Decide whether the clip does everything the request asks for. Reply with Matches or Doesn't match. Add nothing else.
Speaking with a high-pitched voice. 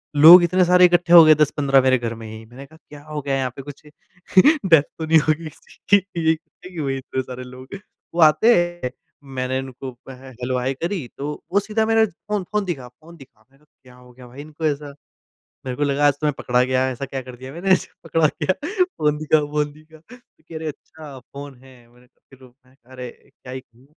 Doesn't match